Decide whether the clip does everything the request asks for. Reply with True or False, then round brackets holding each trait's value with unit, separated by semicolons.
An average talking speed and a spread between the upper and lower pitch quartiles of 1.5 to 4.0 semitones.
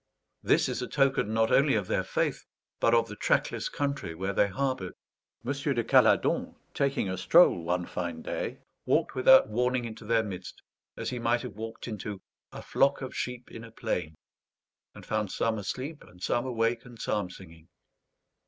False (180 wpm; 4.7 semitones)